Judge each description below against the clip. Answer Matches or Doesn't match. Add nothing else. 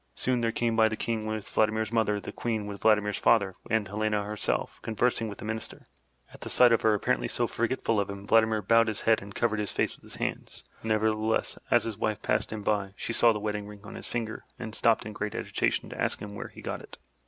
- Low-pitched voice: Matches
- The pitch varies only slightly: Matches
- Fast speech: Matches